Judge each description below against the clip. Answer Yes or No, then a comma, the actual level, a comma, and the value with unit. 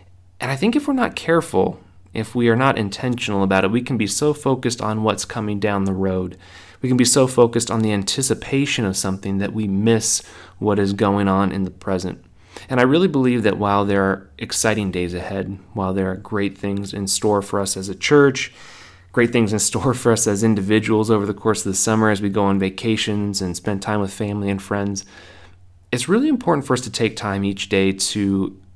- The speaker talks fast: Yes, fast, 220 wpm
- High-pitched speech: No, low, 105 Hz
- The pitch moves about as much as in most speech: Yes, average, 3.4 semitones